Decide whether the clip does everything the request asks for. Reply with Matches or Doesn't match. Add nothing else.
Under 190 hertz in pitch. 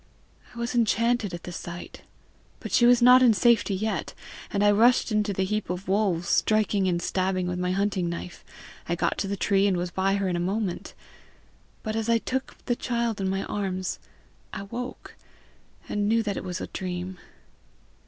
Doesn't match